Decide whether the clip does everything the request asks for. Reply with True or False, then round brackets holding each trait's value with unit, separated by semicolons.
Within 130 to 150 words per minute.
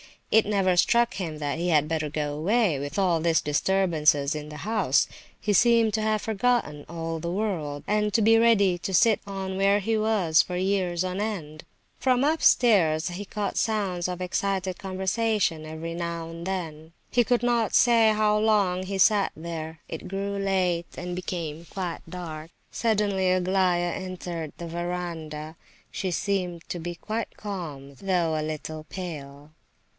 False (165 wpm)